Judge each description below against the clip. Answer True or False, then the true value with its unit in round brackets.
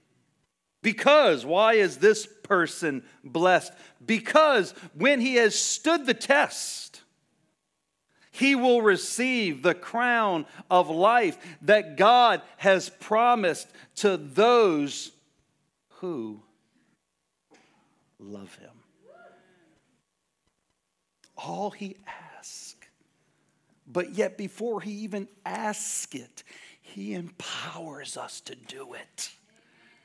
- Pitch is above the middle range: True (205 Hz)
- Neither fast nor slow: False (90 wpm)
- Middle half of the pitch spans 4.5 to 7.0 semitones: True (5.1 semitones)